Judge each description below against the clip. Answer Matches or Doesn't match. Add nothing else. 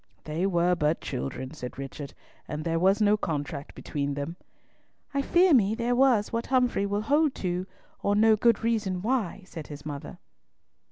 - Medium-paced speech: Matches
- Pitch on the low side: Doesn't match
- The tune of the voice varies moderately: Doesn't match